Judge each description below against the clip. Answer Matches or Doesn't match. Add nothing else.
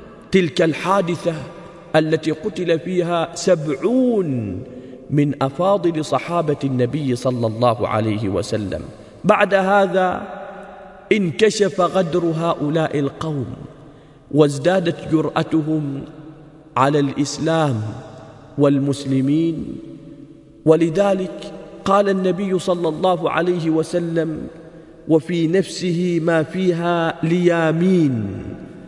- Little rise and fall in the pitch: Doesn't match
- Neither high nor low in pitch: Matches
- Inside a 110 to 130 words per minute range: Doesn't match